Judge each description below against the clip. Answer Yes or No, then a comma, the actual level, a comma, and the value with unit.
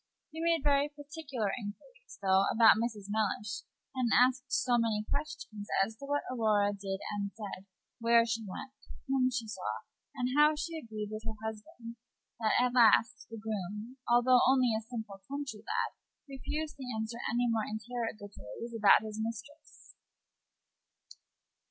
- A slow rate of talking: No, average, 150 wpm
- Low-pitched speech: No, high, 230 Hz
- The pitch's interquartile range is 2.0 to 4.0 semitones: Yes, average, 3.5 semitones